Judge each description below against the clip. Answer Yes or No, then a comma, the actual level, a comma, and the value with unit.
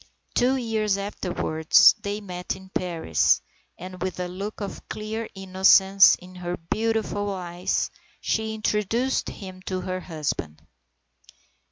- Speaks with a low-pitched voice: No, high, 190 Hz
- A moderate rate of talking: No, slow, 125 wpm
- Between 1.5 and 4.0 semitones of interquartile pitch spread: Yes, average, 2.9 semitones